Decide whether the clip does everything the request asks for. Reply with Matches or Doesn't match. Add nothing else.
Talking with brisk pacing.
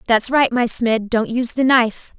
Matches